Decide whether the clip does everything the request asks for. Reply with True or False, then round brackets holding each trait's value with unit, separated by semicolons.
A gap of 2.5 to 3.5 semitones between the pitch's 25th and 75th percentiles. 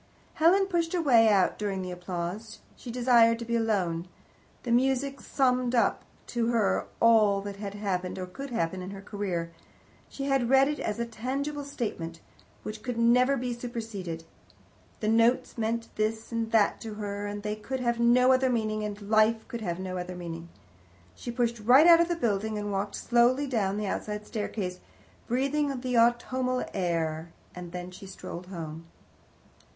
False (4.2 semitones)